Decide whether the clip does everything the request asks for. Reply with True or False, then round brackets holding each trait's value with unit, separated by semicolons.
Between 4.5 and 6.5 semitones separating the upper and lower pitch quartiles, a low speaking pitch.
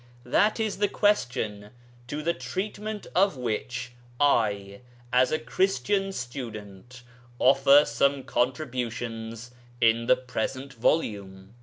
True (5.4 semitones; 125 Hz)